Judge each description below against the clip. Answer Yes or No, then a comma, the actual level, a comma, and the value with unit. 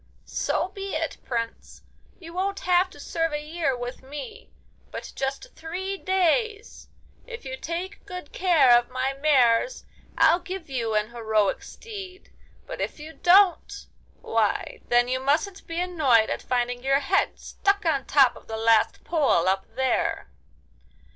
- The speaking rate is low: No, average, 150 wpm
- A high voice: Yes, very high, 305 Hz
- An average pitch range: No, wide, 6.7 semitones